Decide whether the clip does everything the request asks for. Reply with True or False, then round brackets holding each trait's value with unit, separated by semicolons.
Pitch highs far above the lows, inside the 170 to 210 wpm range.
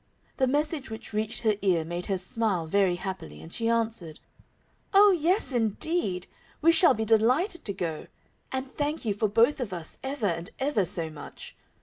True (7.0 semitones; 180 wpm)